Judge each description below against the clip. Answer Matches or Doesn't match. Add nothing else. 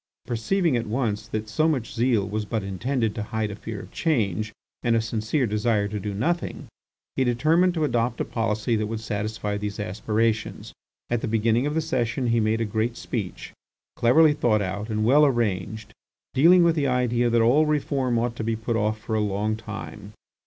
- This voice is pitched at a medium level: Doesn't match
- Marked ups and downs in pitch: Doesn't match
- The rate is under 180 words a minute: Doesn't match